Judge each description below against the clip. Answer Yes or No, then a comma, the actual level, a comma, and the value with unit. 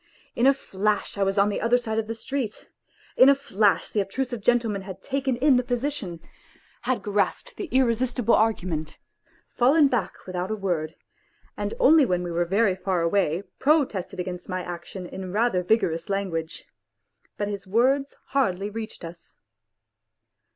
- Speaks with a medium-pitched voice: No, high, 210 Hz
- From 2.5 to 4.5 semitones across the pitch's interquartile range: No, average, 5.2 semitones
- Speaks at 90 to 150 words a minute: No, average, 160 wpm